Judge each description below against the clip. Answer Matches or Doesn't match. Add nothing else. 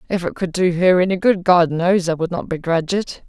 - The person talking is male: Doesn't match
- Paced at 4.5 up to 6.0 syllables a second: Matches